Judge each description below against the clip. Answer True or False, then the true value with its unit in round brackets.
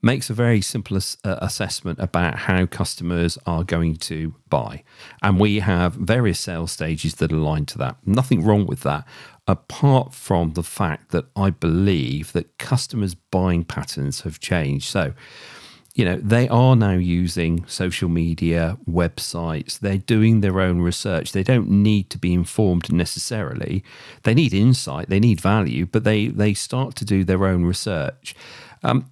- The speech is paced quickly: False (165 wpm)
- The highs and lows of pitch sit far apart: False (4.2 semitones)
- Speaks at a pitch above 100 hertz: False (95 Hz)